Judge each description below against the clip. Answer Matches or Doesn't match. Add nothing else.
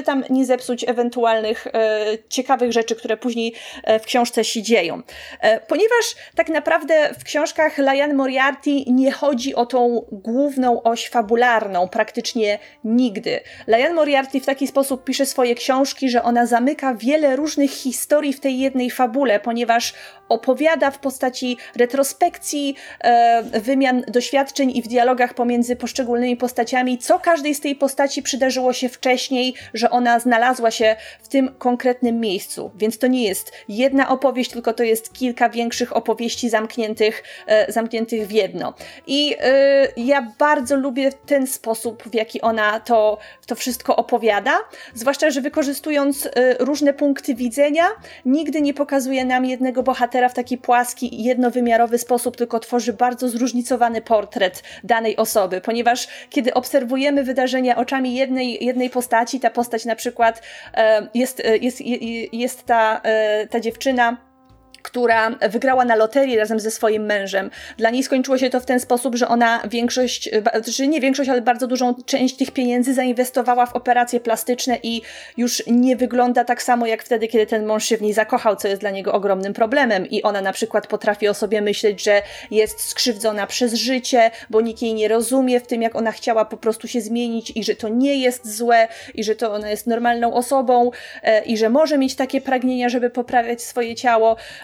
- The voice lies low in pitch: Doesn't match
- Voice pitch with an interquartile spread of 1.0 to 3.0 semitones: Matches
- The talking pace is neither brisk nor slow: Doesn't match